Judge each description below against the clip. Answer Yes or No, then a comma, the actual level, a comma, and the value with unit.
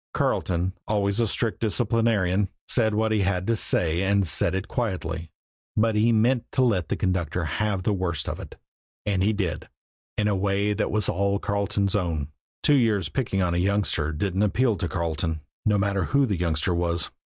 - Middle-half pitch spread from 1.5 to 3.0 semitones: No, average, 3.4 semitones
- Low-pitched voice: Yes, low, 100 Hz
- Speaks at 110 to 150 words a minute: No, average, 185 wpm